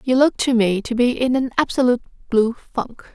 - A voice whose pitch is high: Yes, high, 245 Hz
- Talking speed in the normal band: No, fast, 210 wpm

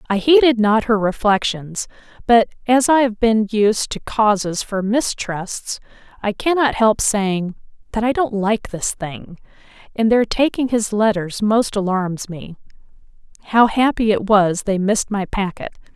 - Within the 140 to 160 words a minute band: Yes, average, 150 wpm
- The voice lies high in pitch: Yes, high, 215 Hz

